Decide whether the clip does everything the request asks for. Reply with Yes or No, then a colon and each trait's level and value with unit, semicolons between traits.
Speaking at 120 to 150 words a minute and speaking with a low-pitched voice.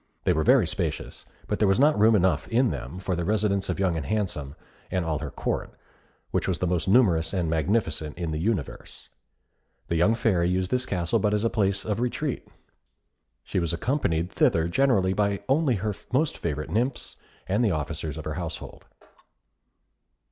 No: average, 185 wpm; very low, 95 Hz